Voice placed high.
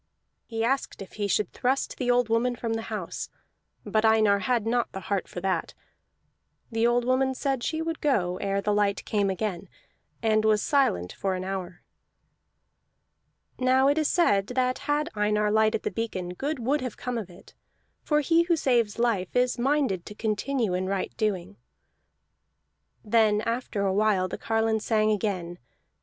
Yes: high, 220 Hz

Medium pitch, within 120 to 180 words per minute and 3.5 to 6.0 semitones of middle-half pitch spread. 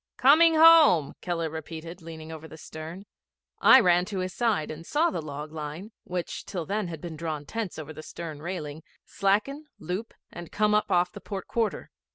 No: medium, 175 Hz; average, 190 wpm; average, 4.9 semitones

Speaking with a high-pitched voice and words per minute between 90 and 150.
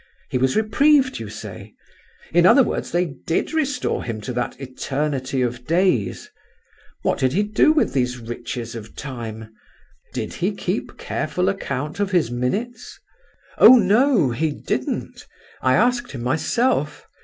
No: medium, 145 Hz; average, 145 wpm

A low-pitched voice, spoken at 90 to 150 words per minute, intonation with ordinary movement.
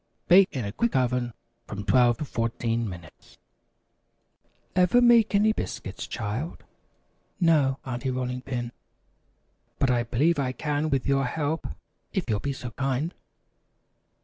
Yes: low, 130 Hz; slow, 135 wpm; average, 4.7 semitones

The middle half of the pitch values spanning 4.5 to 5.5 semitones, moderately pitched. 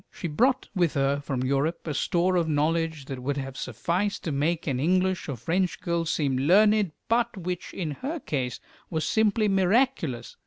Yes: average, 4.9 semitones; medium, 165 Hz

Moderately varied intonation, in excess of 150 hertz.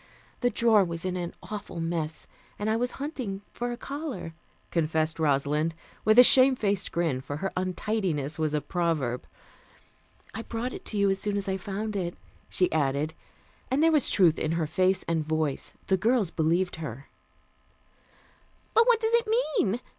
No: wide, 6.1 semitones; medium, 185 Hz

